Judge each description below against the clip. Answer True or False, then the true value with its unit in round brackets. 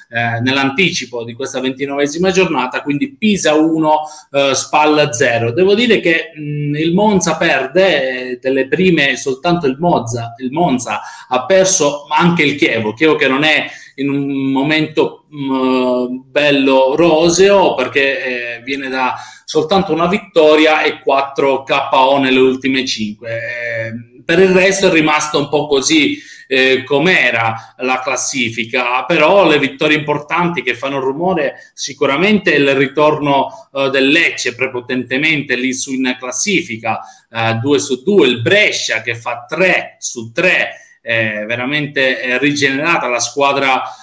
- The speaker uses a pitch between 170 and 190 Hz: False (140 Hz)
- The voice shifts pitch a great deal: False (3.8 semitones)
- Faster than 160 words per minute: False (130 wpm)